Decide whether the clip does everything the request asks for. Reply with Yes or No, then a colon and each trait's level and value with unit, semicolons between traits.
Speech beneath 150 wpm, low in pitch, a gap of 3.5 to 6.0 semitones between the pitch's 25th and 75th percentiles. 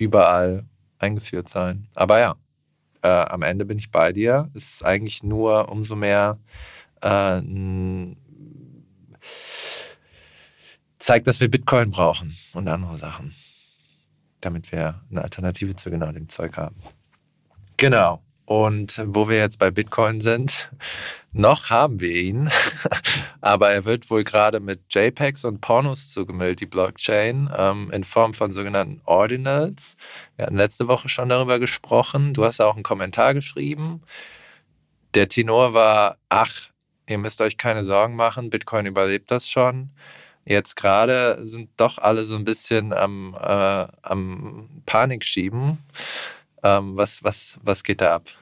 Yes: average, 140 wpm; low, 105 Hz; average, 4.3 semitones